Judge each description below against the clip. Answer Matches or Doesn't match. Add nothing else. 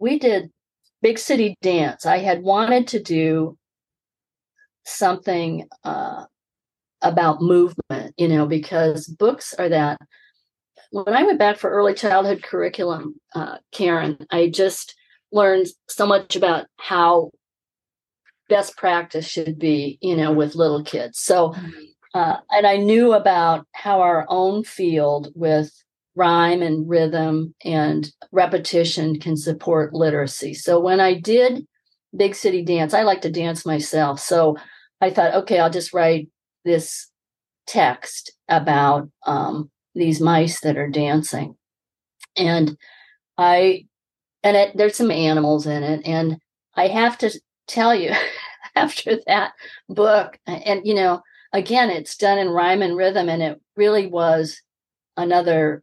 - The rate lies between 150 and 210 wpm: Doesn't match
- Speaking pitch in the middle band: Matches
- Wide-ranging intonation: Doesn't match